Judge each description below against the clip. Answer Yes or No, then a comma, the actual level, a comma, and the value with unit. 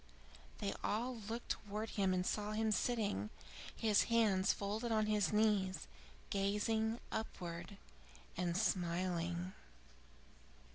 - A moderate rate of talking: No, slow, 105 wpm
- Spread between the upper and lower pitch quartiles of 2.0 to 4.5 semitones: Yes, average, 3.0 semitones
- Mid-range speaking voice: No, high, 205 Hz